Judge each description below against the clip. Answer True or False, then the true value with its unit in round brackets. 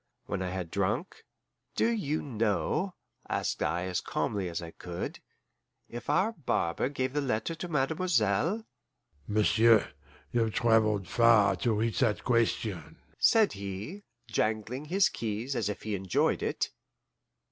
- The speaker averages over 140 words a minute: False (135 wpm)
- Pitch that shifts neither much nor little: False (6.2 semitones)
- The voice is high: False (115 Hz)